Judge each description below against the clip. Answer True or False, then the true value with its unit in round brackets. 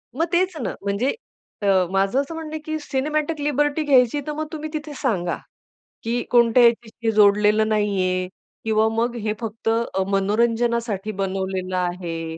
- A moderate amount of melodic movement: False (6.1 semitones)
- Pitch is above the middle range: True (230 Hz)